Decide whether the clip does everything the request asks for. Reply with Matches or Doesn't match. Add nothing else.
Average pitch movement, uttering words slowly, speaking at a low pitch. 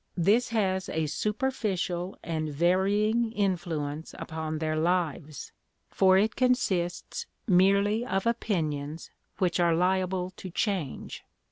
Doesn't match